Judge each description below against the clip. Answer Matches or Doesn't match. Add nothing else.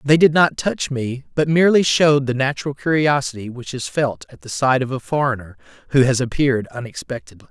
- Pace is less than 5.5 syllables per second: Doesn't match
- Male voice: Matches